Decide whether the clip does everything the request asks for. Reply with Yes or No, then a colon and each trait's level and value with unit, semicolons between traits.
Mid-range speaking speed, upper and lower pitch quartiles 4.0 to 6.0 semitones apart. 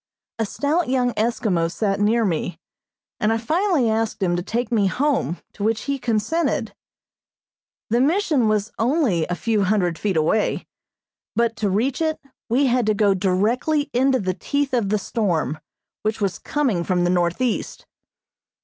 Yes: average, 160 wpm; average, 4.8 semitones